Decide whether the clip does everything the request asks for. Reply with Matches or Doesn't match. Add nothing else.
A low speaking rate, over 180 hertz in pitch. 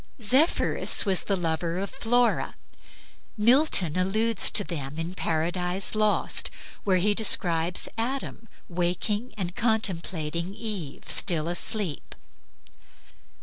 Matches